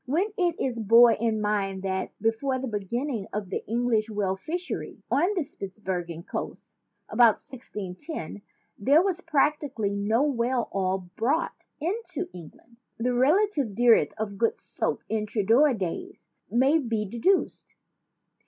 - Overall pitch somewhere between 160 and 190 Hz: No, high, 235 Hz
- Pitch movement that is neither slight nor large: No, wide, 6.0 semitones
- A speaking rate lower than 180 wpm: Yes, average, 145 wpm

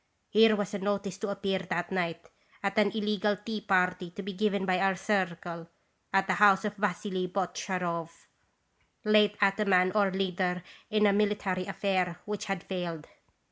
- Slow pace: No, average, 170 wpm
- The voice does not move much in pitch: Yes, narrow, 2.2 semitones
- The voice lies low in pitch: No, high, 195 Hz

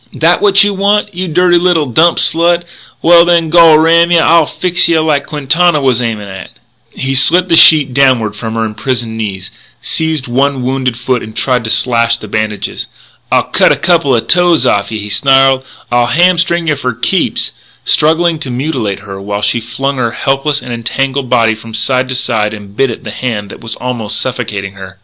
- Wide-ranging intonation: Yes, wide, 6.3 semitones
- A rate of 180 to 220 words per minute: Yes, average, 200 wpm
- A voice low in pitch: Yes, low, 130 Hz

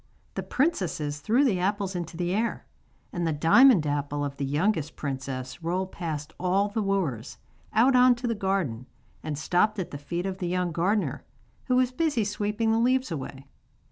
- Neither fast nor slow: Yes, average, 180 wpm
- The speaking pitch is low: No, medium, 180 Hz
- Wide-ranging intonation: Yes, wide, 6.5 semitones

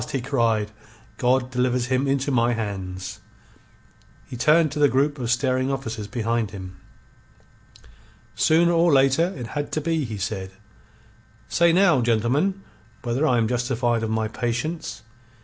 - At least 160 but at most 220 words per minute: No, average, 145 wpm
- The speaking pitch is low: Yes, low, 125 Hz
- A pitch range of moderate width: Yes, average, 4.2 semitones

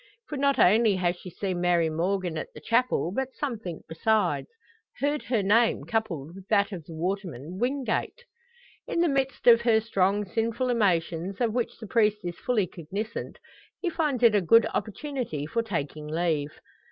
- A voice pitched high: Yes, high, 210 Hz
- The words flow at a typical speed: Yes, average, 170 wpm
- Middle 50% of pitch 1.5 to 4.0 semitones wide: No, average, 5.2 semitones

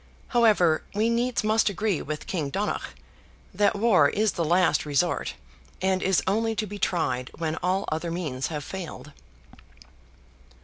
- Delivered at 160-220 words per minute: No, average, 145 wpm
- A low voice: No, medium, 185 Hz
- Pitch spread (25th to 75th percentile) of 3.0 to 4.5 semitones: No, average, 5.1 semitones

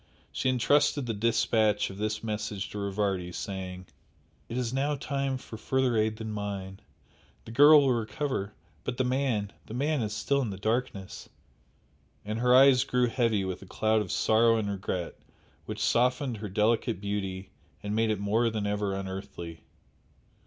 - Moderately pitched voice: No, low, 110 Hz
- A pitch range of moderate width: Yes, average, 3.7 semitones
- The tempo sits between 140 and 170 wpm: Yes, average, 165 wpm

